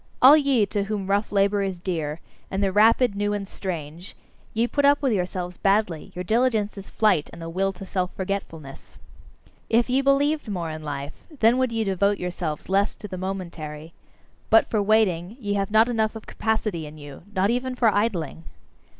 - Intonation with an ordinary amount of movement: Yes, average, 3.8 semitones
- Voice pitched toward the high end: Yes, high, 200 Hz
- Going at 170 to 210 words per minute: Yes, average, 190 wpm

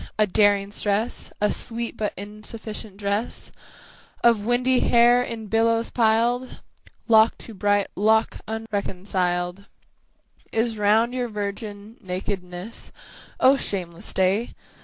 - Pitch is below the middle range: No, high, 215 Hz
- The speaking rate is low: Yes, slow, 110 wpm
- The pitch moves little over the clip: Yes, narrow, 2.3 semitones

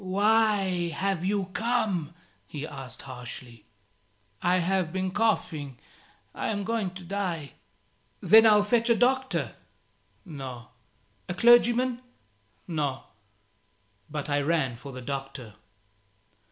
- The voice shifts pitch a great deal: Yes, wide, 7.2 semitones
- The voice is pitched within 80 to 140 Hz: No, medium, 180 Hz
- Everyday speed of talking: No, slow, 115 wpm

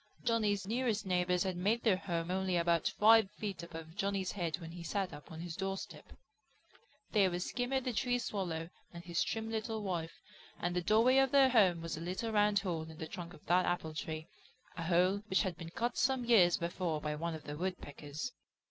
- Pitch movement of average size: Yes, average, 4.1 semitones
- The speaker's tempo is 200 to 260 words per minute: Yes, fast, 205 wpm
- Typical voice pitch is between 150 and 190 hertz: Yes, medium, 185 Hz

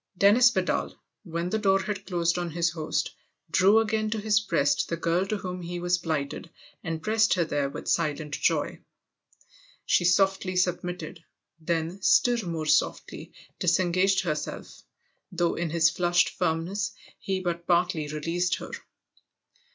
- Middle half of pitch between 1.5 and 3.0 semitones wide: Yes, narrow, 2.6 semitones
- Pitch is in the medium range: Yes, medium, 175 Hz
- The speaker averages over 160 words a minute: No, average, 150 wpm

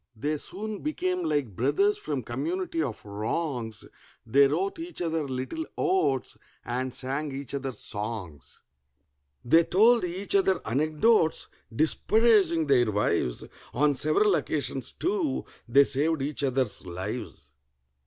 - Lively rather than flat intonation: Yes, wide, 7.0 semitones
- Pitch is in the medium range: Yes, medium, 145 Hz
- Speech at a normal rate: No, slow, 125 wpm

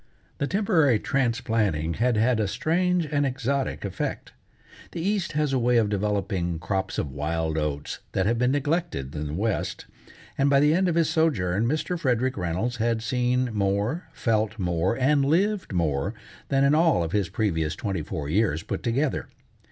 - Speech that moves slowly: No, average, 175 wpm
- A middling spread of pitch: No, wide, 7.2 semitones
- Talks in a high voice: No, low, 115 Hz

